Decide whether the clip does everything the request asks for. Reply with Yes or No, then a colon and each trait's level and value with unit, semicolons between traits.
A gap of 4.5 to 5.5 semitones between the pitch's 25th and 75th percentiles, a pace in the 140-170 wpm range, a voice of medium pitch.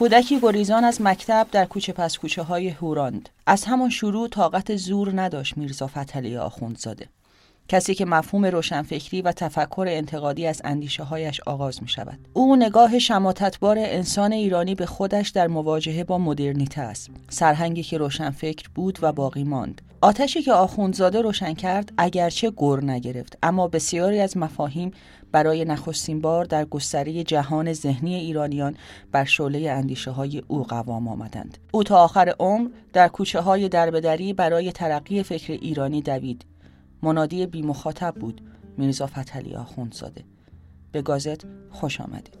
Yes: average, 4.9 semitones; average, 145 wpm; medium, 160 Hz